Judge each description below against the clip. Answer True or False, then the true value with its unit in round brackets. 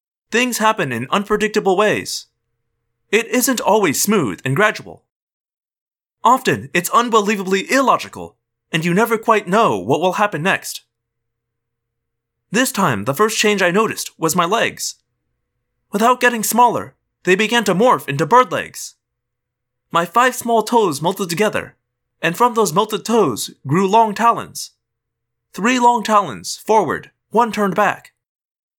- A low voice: False (195 Hz)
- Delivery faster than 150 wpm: False (135 wpm)